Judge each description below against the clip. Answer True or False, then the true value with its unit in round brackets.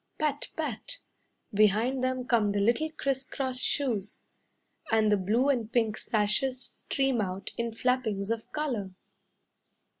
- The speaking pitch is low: False (235 Hz)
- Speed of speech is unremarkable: False (130 wpm)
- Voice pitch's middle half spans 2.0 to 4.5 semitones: True (3.9 semitones)